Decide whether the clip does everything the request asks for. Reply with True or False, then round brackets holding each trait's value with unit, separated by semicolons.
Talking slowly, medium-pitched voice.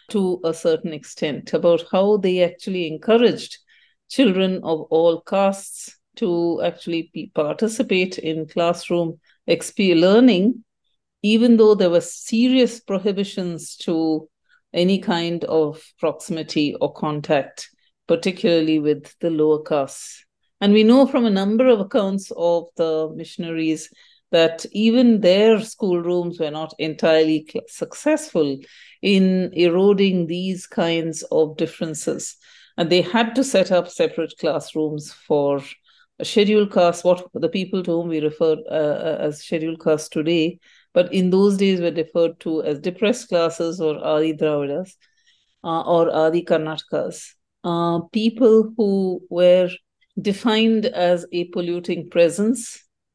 True (130 wpm; 175 Hz)